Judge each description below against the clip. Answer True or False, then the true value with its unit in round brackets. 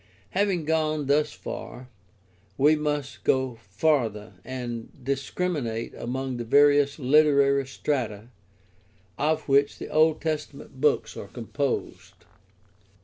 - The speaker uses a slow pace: True (105 wpm)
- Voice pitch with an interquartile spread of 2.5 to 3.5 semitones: True (3.2 semitones)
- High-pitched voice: False (140 Hz)